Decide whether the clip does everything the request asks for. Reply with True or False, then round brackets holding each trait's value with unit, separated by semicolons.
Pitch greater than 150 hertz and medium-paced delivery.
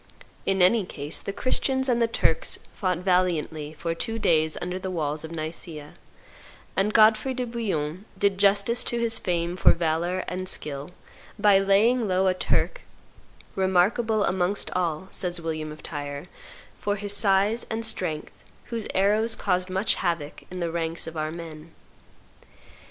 True (185 Hz; 155 wpm)